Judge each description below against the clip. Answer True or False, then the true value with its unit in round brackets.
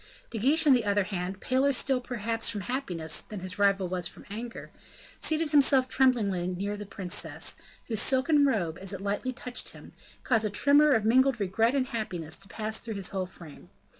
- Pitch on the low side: False (220 Hz)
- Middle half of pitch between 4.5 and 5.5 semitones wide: True (5.0 semitones)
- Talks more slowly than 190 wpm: False (195 wpm)